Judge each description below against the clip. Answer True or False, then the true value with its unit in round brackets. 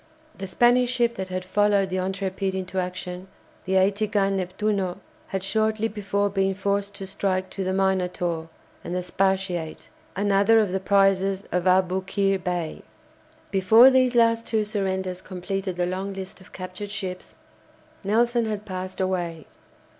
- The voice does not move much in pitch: True (1.6 semitones)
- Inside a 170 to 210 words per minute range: False (150 wpm)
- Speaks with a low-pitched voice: False (195 Hz)